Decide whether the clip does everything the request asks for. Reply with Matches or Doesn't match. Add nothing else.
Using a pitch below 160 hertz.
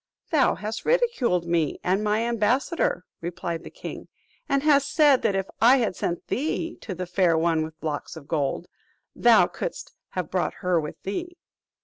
Doesn't match